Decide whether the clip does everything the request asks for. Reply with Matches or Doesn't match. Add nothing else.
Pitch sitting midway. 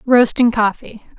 Doesn't match